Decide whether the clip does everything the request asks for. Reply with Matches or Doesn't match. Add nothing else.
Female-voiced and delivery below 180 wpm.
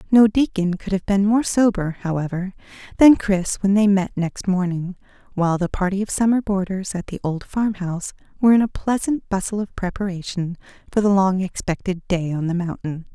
Doesn't match